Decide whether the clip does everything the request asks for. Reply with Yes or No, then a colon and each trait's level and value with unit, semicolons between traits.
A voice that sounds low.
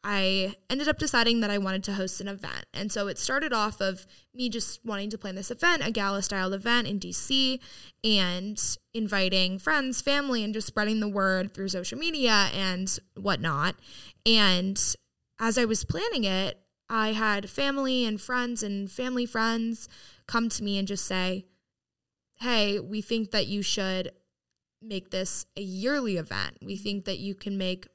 No: high, 205 Hz